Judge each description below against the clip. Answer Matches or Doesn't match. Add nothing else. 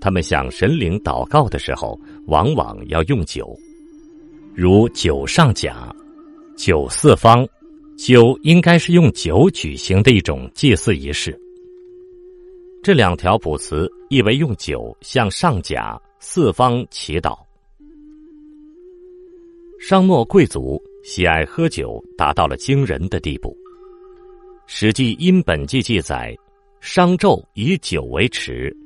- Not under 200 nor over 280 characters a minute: Doesn't match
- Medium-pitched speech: Doesn't match